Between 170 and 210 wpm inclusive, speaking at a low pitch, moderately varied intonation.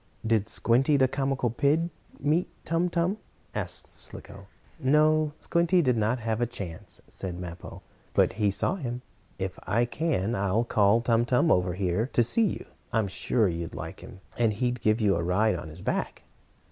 No: average, 175 wpm; low, 115 Hz; wide, 6.0 semitones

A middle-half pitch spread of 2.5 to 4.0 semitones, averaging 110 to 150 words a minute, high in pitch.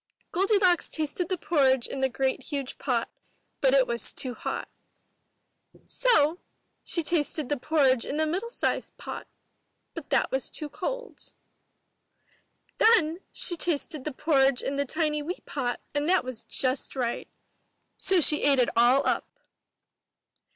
No: average, 4.4 semitones; average, 145 wpm; very high, 295 Hz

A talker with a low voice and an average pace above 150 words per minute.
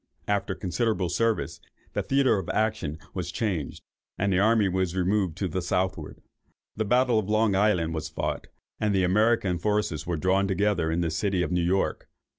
Yes: very low, 95 Hz; average, 180 wpm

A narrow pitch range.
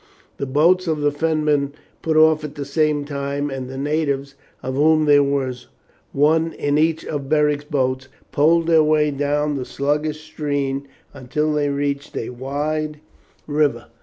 Yes: narrow, 1.7 semitones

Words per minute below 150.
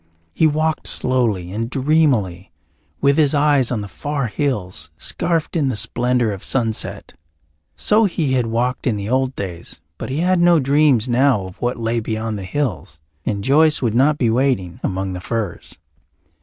No: average, 170 wpm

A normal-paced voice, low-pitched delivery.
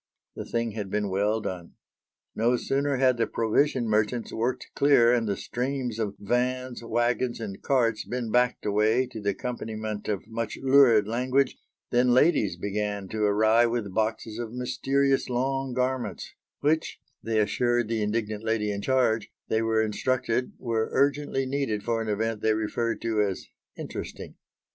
Yes: average, 160 wpm; low, 115 Hz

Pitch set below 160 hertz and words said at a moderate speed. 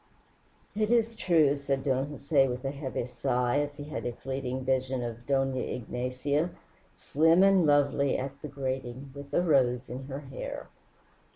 Yes: low, 135 Hz; average, 165 wpm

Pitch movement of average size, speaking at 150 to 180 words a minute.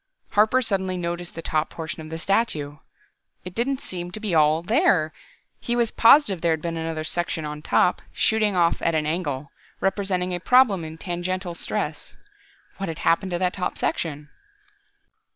Yes: average, 3.5 semitones; average, 170 wpm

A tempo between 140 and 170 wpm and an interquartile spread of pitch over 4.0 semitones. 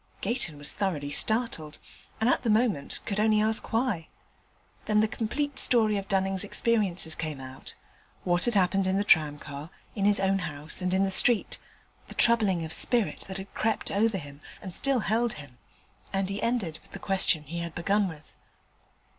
No: average, 180 wpm; average, 5.1 semitones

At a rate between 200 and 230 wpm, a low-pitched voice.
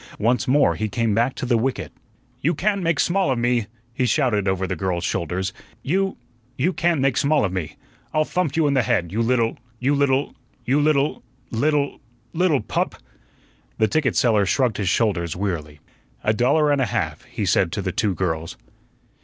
No: average, 185 wpm; low, 120 Hz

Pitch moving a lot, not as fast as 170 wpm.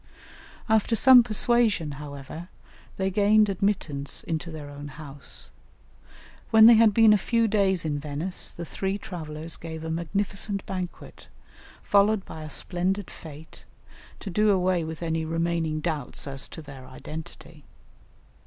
No: average, 4.7 semitones; average, 140 wpm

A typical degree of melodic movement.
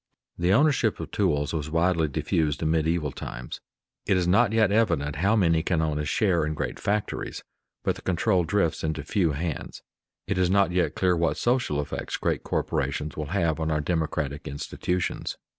Yes: average, 3.7 semitones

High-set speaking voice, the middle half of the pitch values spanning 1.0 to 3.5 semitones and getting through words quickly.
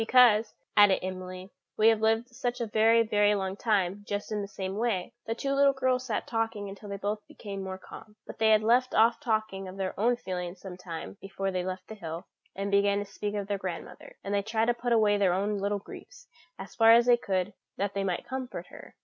Yes: high, 205 Hz; average, 2.8 semitones; fast, 230 wpm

